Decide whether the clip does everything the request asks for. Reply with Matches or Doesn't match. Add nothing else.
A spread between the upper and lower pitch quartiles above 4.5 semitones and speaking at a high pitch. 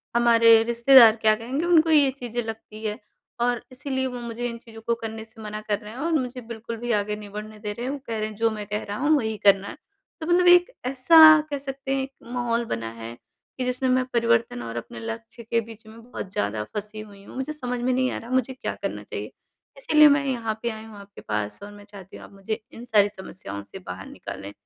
Doesn't match